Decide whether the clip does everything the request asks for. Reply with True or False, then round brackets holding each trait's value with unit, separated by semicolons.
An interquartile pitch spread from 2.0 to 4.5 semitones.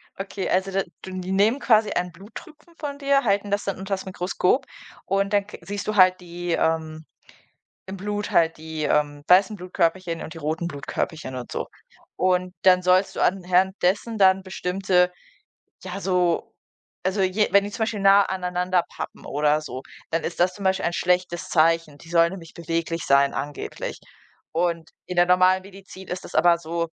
True (2.6 semitones)